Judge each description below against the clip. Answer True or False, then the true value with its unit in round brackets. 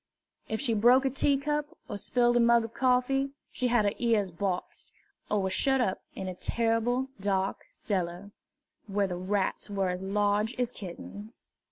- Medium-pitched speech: False (220 Hz)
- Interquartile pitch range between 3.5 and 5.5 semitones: True (4.3 semitones)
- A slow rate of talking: False (170 wpm)